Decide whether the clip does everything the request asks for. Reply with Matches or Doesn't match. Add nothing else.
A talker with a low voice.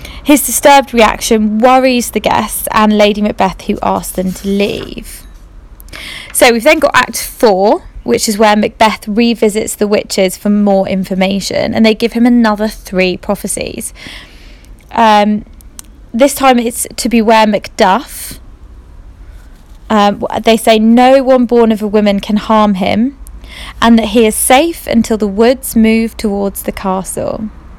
Doesn't match